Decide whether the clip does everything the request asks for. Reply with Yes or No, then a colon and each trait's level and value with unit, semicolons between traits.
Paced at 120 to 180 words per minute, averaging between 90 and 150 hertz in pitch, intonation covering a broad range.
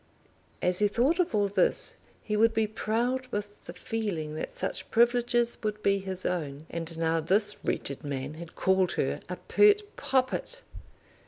No: average, 165 wpm; high, 205 Hz; wide, 5.7 semitones